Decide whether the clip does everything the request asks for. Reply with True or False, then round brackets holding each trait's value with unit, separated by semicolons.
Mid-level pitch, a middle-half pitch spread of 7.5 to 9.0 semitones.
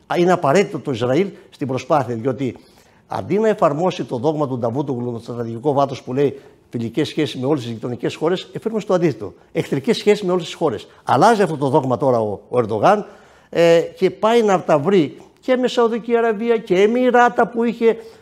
True (165 Hz; 7.8 semitones)